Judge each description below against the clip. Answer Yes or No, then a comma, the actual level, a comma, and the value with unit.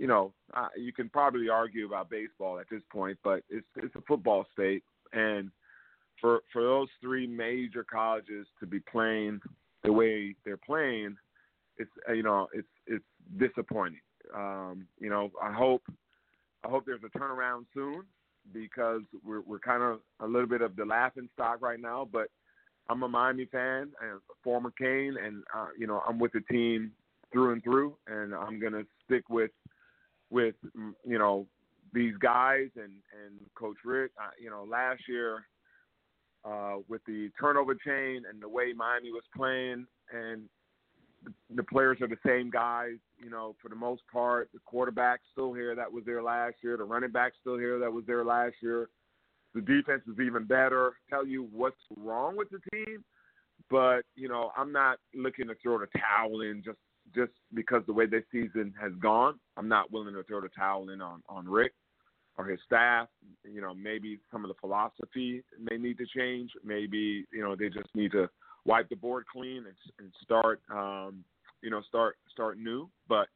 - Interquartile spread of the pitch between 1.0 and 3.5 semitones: Yes, average, 2.8 semitones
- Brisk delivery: No, average, 185 wpm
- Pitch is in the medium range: No, low, 115 Hz